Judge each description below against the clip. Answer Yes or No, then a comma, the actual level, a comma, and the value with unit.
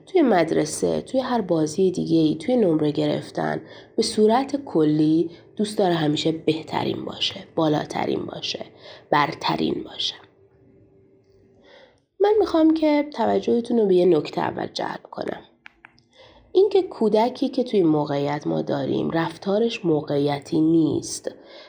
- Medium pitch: Yes, medium, 170 Hz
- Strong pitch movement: Yes, wide, 8.2 semitones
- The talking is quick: No, average, 120 wpm